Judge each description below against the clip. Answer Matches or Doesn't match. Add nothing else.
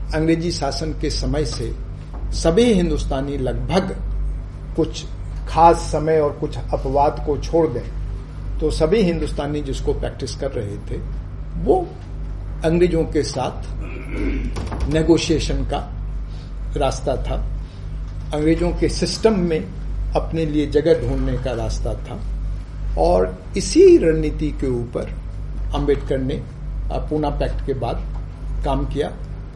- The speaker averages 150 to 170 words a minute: Doesn't match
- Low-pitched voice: Doesn't match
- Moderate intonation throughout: Doesn't match